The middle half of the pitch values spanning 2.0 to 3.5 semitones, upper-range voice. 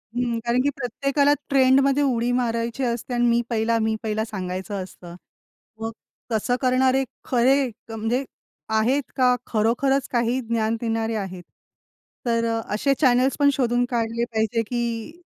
Yes: narrow, 2.5 semitones; high, 235 Hz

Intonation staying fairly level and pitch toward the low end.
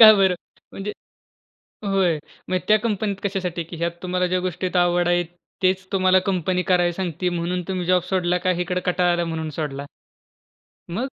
No: narrow, 1.3 semitones; medium, 180 Hz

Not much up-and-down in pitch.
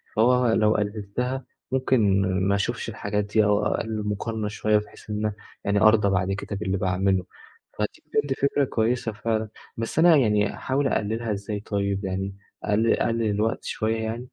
Yes: narrow, 2.1 semitones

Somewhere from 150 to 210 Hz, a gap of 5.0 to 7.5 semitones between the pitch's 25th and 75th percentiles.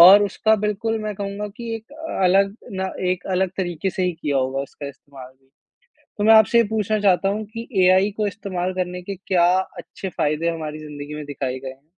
Yes: medium, 185 Hz; average, 5.3 semitones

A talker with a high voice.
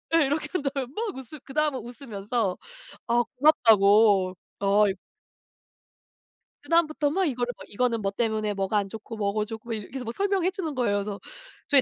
Yes: high, 240 Hz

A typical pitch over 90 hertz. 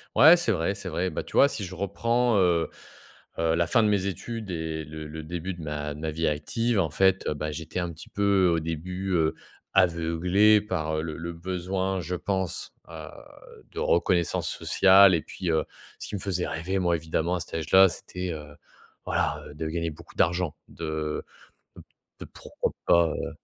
No: very low, 85 Hz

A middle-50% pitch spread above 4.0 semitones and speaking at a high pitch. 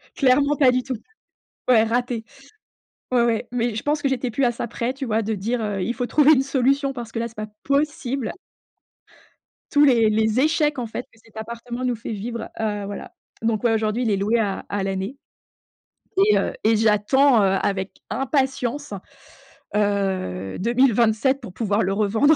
No: average, 3.7 semitones; high, 235 Hz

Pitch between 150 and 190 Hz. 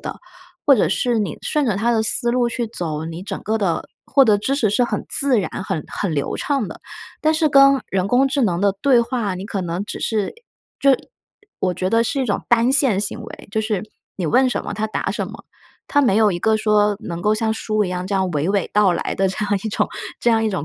No: high, 215 Hz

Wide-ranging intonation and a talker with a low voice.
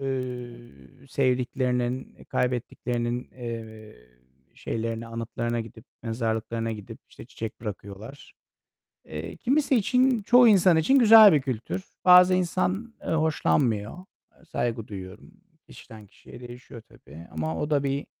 Yes: wide, 6.2 semitones; low, 120 Hz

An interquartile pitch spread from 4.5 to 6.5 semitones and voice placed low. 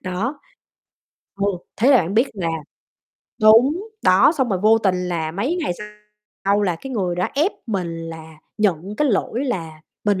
No: average, 5.2 semitones; high, 200 Hz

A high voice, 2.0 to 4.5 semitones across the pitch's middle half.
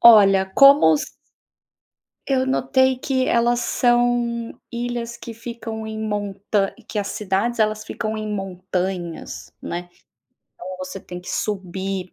Yes: high, 215 Hz; average, 3.7 semitones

